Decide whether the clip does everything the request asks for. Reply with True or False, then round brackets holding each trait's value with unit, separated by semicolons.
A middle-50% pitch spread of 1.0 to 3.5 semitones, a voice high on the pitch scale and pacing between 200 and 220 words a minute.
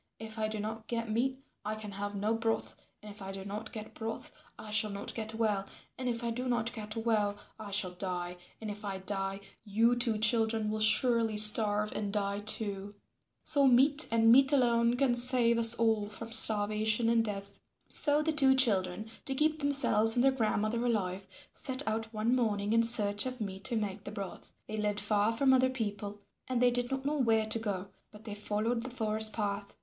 True (2.5 semitones; 220 Hz; 205 wpm)